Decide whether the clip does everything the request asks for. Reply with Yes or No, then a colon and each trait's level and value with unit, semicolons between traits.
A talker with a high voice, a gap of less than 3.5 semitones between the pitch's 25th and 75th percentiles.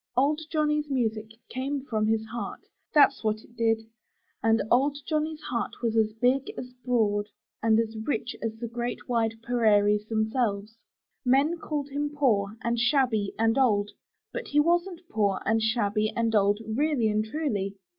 No: high, 230 Hz; average, 4.0 semitones